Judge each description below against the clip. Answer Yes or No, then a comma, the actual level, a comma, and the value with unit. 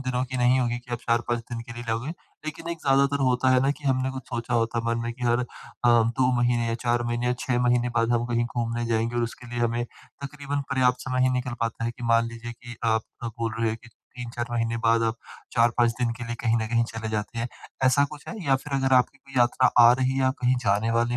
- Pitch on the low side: Yes, low, 120 Hz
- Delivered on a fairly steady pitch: Yes, narrow, 1.7 semitones